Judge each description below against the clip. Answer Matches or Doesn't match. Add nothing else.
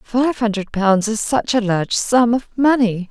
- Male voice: Doesn't match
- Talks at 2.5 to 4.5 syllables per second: Matches